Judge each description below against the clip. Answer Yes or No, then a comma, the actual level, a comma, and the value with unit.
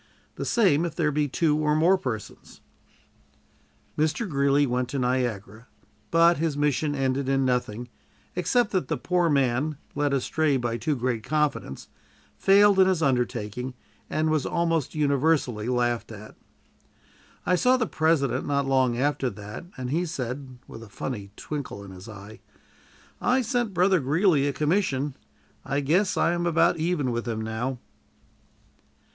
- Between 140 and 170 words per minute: Yes, average, 150 wpm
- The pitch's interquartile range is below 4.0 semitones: No, average, 4.8 semitones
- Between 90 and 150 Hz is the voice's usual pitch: Yes, medium, 140 Hz